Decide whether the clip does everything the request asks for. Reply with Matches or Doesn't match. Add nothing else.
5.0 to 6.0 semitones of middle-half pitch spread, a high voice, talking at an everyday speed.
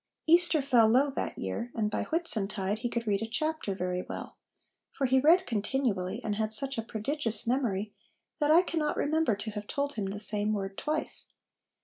Matches